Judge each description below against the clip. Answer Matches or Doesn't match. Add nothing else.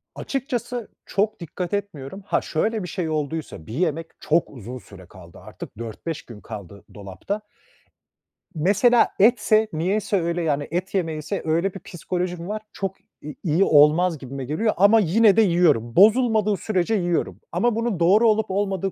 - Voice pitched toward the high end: Doesn't match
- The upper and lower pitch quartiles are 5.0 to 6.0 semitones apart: Matches